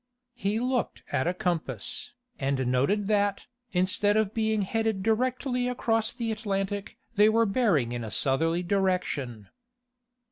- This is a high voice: Yes, high, 200 Hz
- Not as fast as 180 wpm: Yes, slow, 135 wpm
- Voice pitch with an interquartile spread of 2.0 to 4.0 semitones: No, average, 5.2 semitones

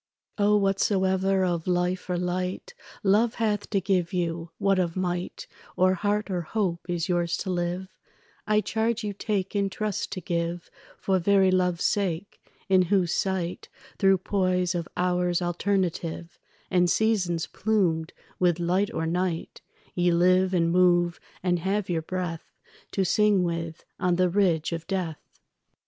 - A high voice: No, medium, 180 Hz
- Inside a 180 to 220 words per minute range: No, average, 150 wpm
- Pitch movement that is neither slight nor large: No, narrow, 2.0 semitones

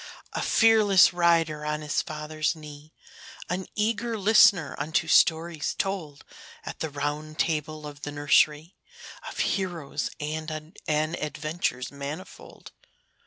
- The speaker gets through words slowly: Yes, slow, 115 wpm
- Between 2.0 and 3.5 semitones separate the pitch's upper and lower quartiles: Yes, average, 2.8 semitones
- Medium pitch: Yes, medium, 155 Hz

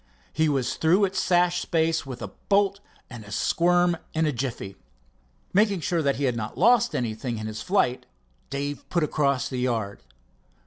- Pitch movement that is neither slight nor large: No, wide, 6.1 semitones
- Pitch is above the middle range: No, medium, 145 Hz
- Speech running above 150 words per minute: Yes, average, 170 wpm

